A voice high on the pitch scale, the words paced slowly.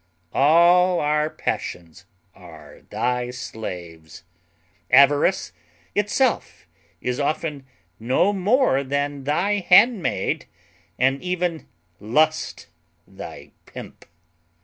No: medium, 145 Hz; slow, 80 wpm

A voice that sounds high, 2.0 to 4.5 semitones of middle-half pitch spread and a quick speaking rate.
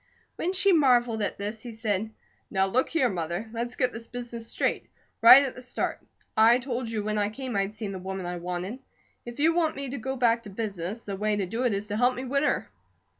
Yes: high, 230 Hz; average, 3.8 semitones; fast, 235 wpm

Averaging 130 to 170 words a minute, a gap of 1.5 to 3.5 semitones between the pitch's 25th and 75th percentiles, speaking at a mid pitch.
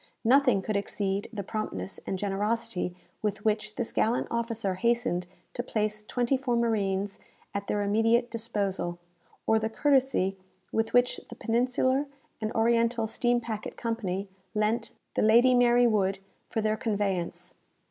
No: average, 140 wpm; average, 2.8 semitones; high, 220 Hz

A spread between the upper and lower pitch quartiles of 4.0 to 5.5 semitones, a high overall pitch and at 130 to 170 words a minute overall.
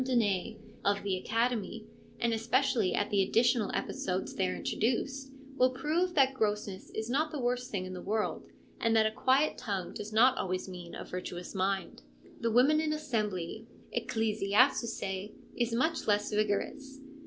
Yes: average, 4.4 semitones; high, 225 Hz; average, 155 wpm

